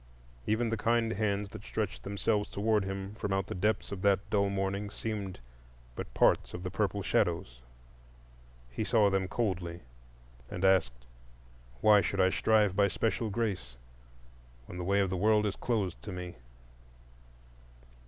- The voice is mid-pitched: No, low, 100 Hz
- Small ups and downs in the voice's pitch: Yes, narrow, 2.3 semitones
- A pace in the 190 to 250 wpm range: No, average, 155 wpm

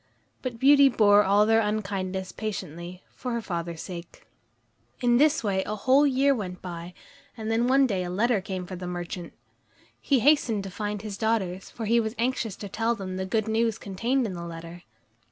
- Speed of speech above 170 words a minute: Yes, average, 190 wpm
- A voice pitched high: Yes, high, 210 Hz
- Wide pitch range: No, average, 4.0 semitones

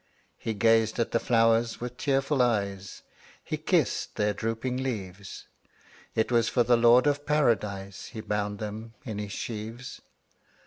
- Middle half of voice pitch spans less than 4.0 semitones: Yes, average, 2.7 semitones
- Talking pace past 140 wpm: Yes, average, 150 wpm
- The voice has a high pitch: No, low, 115 Hz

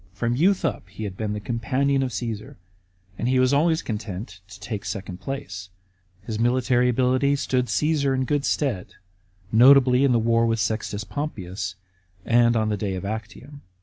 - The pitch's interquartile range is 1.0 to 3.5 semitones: No, average, 4.3 semitones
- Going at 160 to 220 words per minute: Yes, average, 180 wpm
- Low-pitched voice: Yes, low, 115 Hz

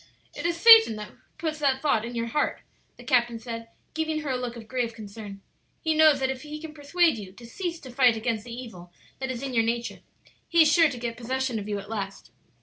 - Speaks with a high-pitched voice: Yes, very high, 250 Hz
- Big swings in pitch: No, average, 5.0 semitones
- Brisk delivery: Yes, fast, 240 wpm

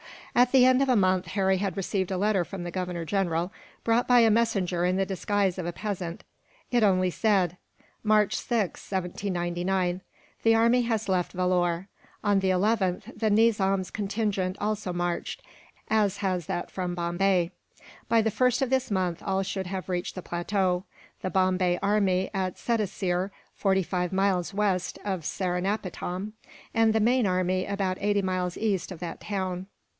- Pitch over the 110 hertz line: Yes, high, 190 Hz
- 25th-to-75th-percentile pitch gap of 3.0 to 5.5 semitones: No, narrow, 2.5 semitones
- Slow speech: No, average, 165 wpm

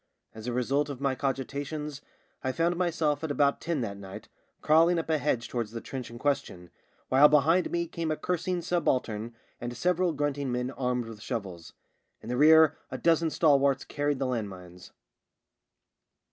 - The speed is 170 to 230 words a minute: Yes, average, 175 wpm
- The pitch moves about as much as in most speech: Yes, average, 4.7 semitones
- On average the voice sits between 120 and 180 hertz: Yes, medium, 140 Hz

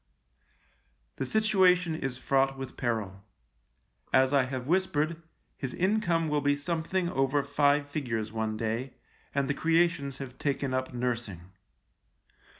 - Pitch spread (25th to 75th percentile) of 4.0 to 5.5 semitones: Yes, average, 4.3 semitones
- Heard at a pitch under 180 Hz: Yes, medium, 140 Hz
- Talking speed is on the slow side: Yes, slow, 130 wpm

